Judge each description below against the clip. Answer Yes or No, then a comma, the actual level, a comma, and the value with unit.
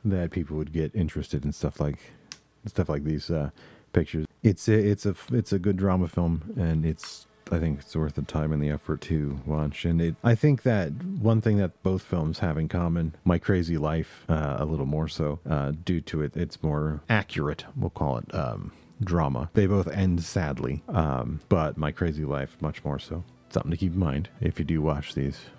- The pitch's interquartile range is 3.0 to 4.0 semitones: Yes, average, 3.6 semitones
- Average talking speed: No, fast, 210 wpm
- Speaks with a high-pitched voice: No, very low, 80 Hz